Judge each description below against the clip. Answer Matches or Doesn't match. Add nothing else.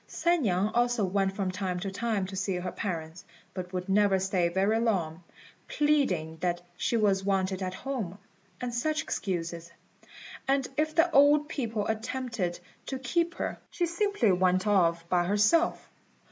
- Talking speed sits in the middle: Matches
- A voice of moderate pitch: Doesn't match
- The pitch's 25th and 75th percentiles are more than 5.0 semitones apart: Matches